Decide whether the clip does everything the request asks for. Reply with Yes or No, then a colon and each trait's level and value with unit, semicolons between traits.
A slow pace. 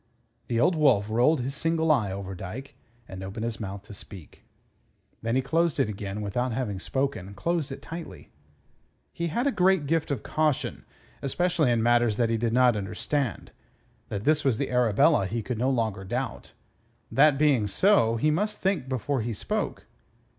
No: average, 175 wpm